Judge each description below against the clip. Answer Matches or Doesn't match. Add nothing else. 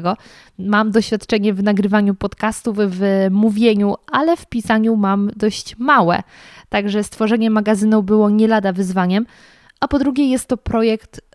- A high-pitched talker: Matches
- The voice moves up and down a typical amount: Doesn't match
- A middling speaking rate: Matches